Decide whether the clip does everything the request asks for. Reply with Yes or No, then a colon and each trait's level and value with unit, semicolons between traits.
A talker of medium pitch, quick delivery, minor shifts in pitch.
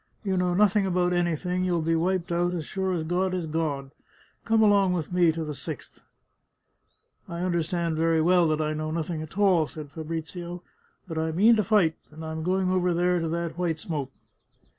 Yes: medium, 170 Hz; fast, 210 wpm; narrow, 2.3 semitones